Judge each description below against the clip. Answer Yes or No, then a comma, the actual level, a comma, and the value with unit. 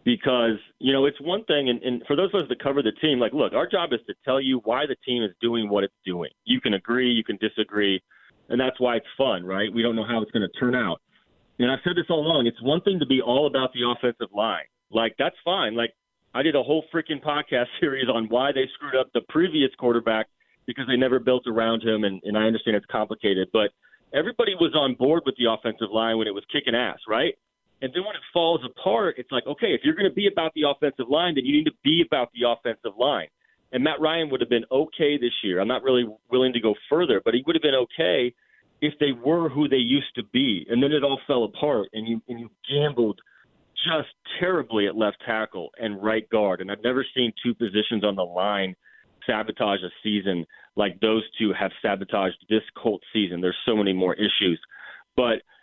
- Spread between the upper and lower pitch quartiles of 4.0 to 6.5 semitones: Yes, average, 4.7 semitones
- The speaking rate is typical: No, fast, 235 wpm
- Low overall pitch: Yes, low, 120 Hz